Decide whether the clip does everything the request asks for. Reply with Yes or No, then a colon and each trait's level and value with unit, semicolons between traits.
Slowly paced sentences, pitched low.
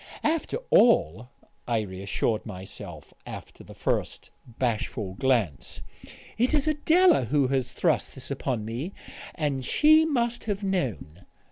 Yes: slow, 125 wpm; low, 130 Hz